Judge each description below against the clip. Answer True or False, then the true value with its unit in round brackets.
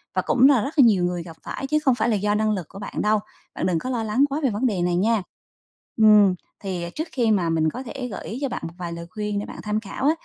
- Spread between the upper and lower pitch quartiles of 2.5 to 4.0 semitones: False (5.3 semitones)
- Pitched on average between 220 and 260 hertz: False (210 Hz)